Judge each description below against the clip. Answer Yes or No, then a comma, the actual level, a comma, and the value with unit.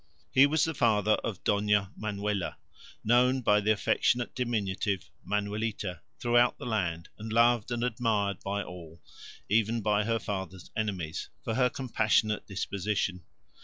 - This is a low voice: Yes, low, 105 Hz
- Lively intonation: No, average, 2.8 semitones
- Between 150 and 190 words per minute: No, slow, 135 wpm